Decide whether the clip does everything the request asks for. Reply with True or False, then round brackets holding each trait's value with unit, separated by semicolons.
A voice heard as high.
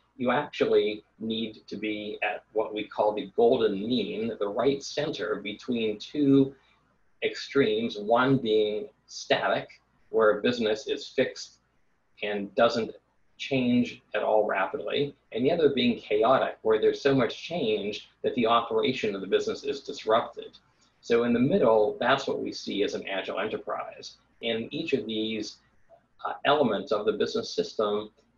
False (135 Hz)